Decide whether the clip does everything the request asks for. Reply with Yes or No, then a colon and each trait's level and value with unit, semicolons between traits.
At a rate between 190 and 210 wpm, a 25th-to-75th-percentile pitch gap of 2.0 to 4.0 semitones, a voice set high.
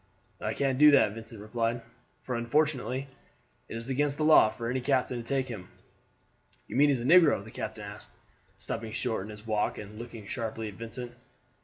No: average, 195 wpm; average, 3.5 semitones; low, 120 Hz